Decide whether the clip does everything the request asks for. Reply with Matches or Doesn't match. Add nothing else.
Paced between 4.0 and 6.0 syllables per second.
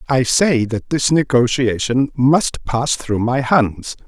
Doesn't match